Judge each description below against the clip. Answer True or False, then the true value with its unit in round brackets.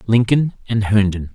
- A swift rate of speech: False (135 wpm)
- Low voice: True (110 Hz)